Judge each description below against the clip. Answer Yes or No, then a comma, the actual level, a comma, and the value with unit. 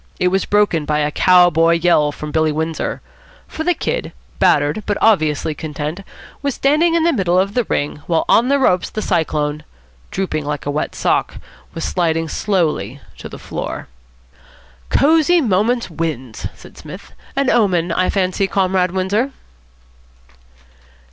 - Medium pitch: Yes, medium, 180 Hz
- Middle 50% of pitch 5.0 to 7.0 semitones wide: Yes, wide, 5.6 semitones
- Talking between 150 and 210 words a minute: Yes, average, 155 wpm